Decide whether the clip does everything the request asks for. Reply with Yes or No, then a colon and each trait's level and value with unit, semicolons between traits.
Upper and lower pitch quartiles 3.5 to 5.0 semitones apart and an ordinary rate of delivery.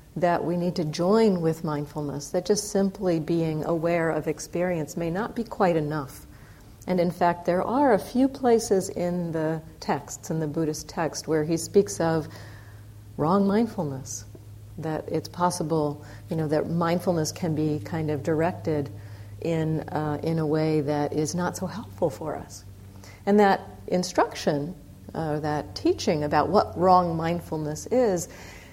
No: average, 3.1 semitones; average, 160 wpm